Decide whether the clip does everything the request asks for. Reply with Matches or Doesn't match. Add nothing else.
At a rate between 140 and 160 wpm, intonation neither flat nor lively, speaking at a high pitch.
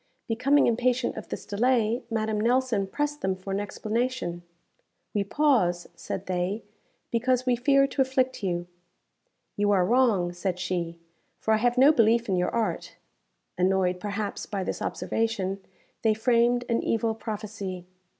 Matches